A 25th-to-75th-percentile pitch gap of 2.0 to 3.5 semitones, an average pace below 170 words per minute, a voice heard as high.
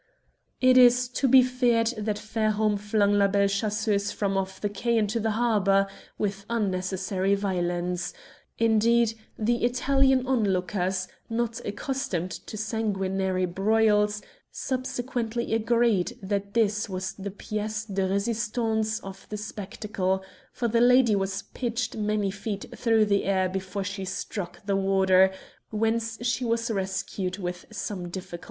Yes: average, 3.0 semitones; slow, 135 wpm; high, 210 Hz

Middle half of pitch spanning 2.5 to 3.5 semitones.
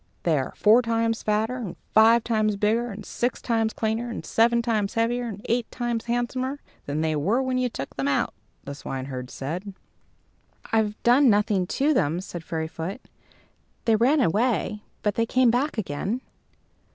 No: average, 4.1 semitones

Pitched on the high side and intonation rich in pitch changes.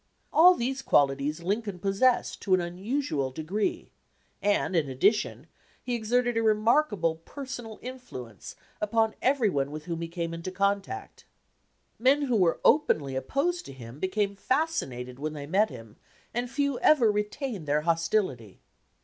Yes: high, 200 Hz; wide, 8.0 semitones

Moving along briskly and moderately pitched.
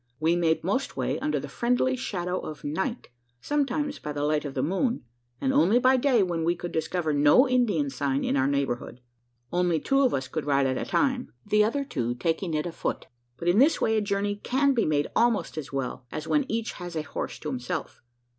Yes: fast, 215 wpm; medium, 175 Hz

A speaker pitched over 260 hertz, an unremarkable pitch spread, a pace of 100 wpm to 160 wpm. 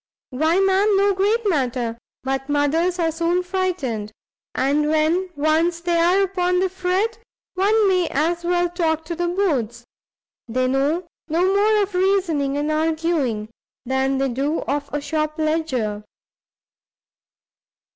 Yes: very high, 330 Hz; average, 4.5 semitones; slow, 135 wpm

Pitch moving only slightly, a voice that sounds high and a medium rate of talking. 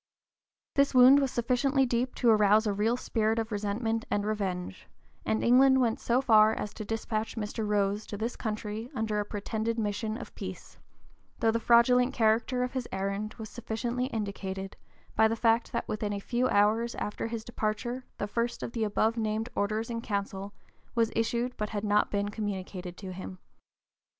Yes: narrow, 2.3 semitones; high, 220 Hz; average, 185 wpm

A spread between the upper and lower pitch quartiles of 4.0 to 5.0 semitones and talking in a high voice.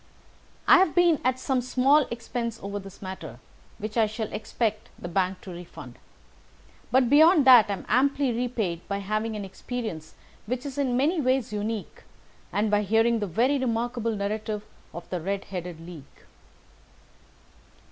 Yes: average, 4.3 semitones; high, 225 Hz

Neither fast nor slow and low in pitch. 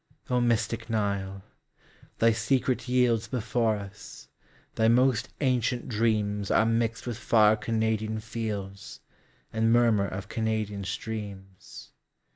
No: slow, 95 wpm; low, 110 Hz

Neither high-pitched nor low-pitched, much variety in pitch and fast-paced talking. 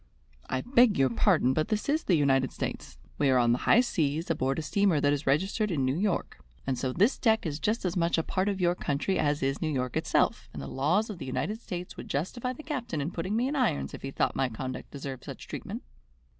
Yes: medium, 160 Hz; wide, 7.3 semitones; fast, 245 wpm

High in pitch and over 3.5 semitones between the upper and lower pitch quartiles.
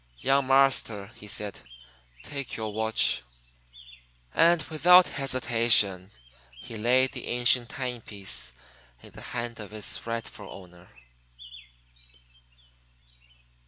No: low, 115 Hz; average, 3.9 semitones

